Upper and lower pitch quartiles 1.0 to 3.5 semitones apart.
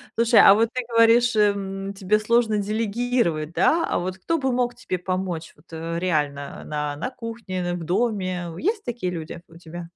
No: average, 5.2 semitones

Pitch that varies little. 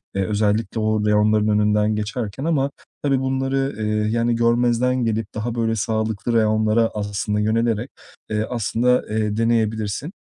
Yes: narrow, 2.0 semitones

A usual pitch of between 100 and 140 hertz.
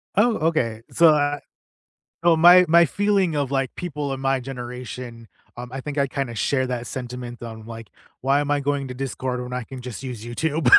Yes: low, 135 Hz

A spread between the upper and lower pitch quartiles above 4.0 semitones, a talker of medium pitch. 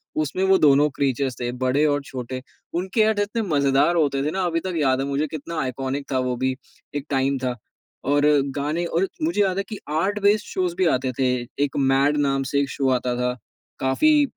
Yes: average, 4.6 semitones; medium, 145 Hz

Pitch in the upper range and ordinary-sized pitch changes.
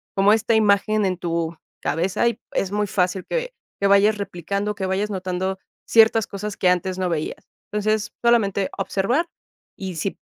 No: high, 200 Hz; narrow, 2.2 semitones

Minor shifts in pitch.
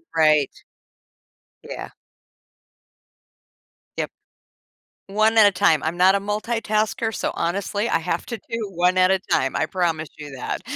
No: average, 4.4 semitones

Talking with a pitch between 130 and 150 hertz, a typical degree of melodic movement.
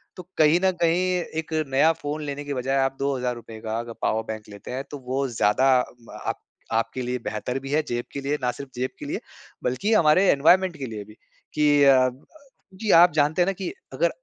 Yes: medium, 140 Hz; average, 4.0 semitones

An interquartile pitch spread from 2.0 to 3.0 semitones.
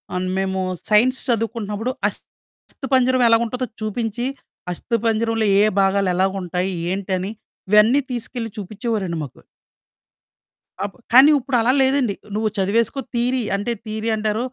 No: average, 3.5 semitones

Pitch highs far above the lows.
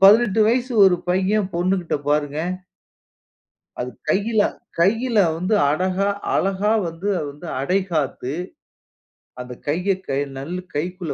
No: average, 3.8 semitones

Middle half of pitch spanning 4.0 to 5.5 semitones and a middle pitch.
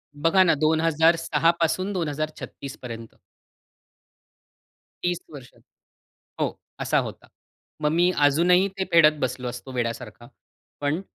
Yes: average, 4.3 semitones; medium, 155 Hz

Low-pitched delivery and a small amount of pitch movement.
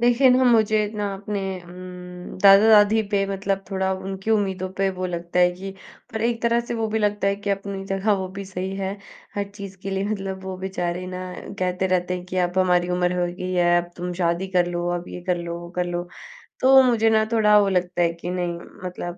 No: high, 190 Hz; narrow, 2.3 semitones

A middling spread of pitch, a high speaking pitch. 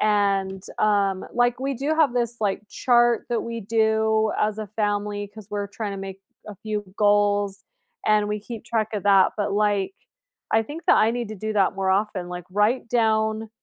No: narrow, 1.9 semitones; high, 210 Hz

